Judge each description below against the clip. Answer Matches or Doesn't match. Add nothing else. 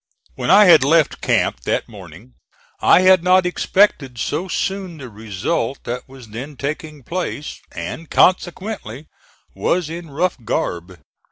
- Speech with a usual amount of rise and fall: Doesn't match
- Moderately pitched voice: Matches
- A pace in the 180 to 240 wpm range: Doesn't match